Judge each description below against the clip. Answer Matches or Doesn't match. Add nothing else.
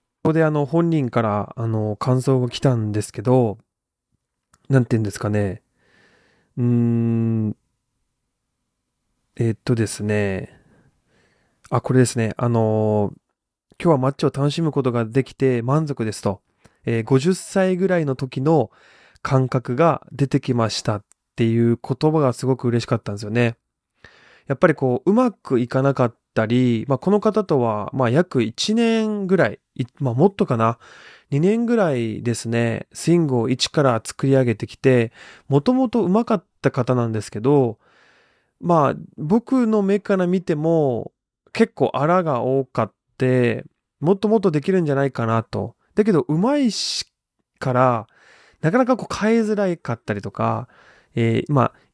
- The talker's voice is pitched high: Doesn't match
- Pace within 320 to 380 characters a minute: Doesn't match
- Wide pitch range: Matches